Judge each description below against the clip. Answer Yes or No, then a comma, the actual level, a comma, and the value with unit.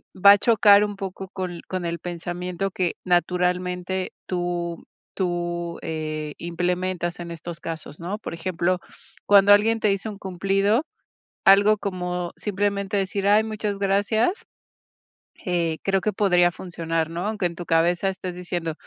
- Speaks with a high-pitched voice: No, medium, 180 Hz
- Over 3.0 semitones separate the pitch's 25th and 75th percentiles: No, narrow, 2.5 semitones